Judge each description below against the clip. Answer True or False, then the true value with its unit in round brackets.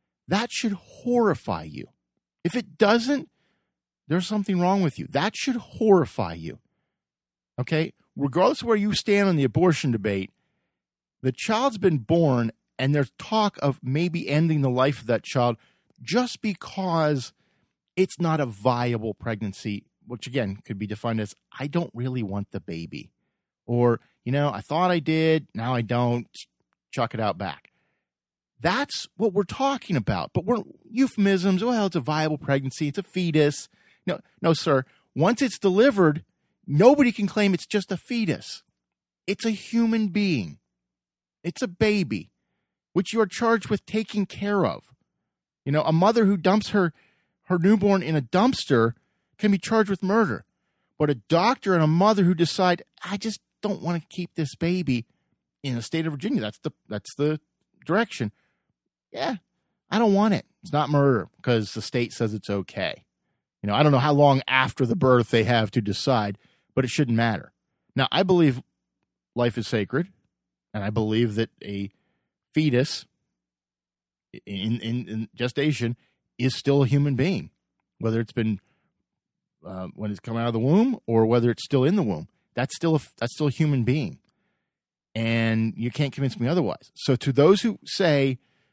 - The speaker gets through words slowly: False (170 wpm)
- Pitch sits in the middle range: True (150 Hz)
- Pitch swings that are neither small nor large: False (8.6 semitones)